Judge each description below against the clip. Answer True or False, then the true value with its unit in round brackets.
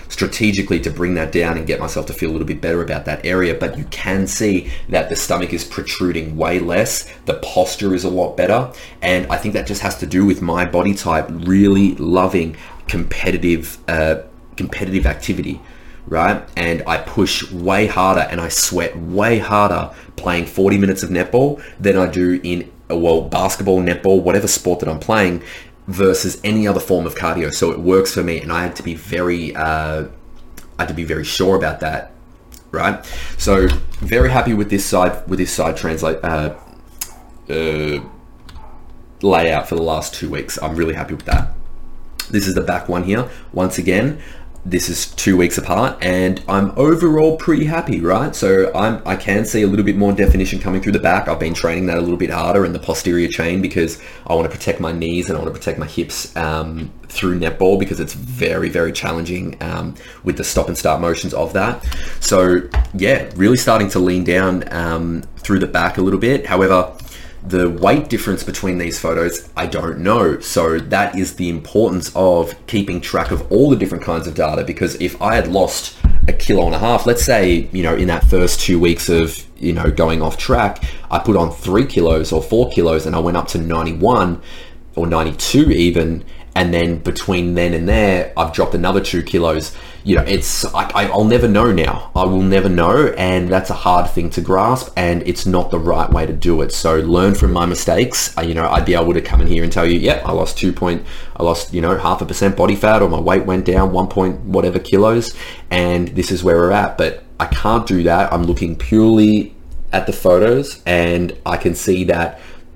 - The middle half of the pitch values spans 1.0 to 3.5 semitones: True (2.6 semitones)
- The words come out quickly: True (210 wpm)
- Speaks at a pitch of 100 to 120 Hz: False (90 Hz)